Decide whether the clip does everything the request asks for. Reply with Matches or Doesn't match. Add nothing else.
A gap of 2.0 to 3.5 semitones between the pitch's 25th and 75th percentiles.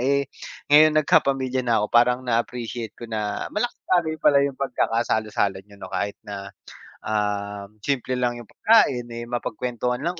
Doesn't match